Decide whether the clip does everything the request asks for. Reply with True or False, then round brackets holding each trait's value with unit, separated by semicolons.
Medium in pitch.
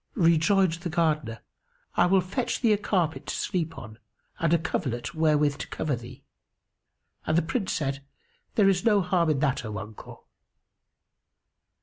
True (165 Hz)